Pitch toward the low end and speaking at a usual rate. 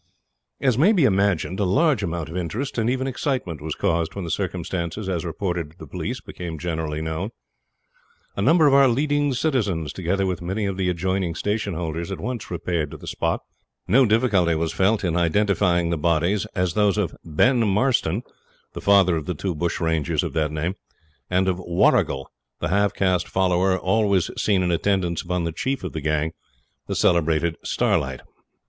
Yes: very low, 90 Hz; average, 185 wpm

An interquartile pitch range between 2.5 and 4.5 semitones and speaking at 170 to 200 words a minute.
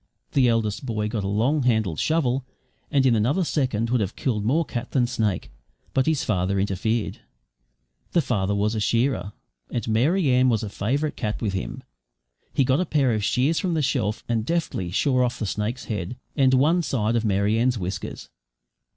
Yes: average, 4.1 semitones; average, 190 wpm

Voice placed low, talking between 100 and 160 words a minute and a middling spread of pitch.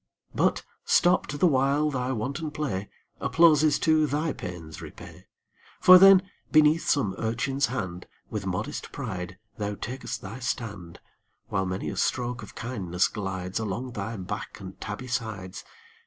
No: low, 120 Hz; average, 140 wpm; wide, 7.2 semitones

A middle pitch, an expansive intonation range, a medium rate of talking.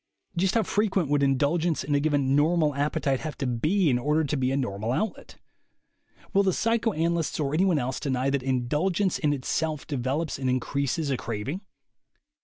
No: medium, 145 Hz; average, 4.1 semitones; average, 180 wpm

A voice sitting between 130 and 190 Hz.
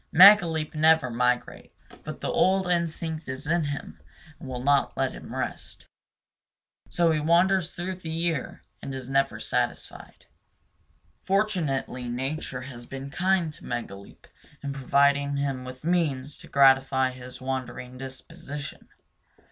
Yes: medium, 140 Hz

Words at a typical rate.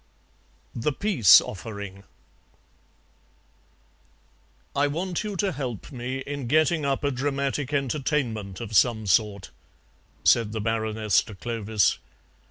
No: slow, 110 wpm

